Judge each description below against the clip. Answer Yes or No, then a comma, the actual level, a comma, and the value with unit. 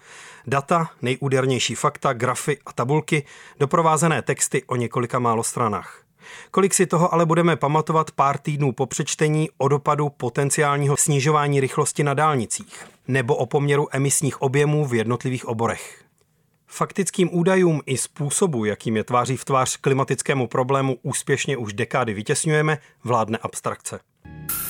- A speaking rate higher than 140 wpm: No, average, 130 wpm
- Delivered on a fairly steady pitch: No, average, 3.4 semitones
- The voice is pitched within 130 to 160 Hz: Yes, medium, 140 Hz